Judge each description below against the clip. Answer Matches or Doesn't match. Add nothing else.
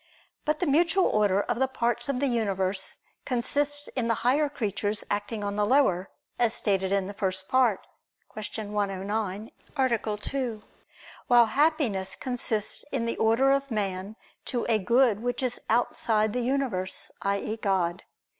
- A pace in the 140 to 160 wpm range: Matches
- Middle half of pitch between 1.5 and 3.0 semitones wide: Doesn't match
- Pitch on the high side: Matches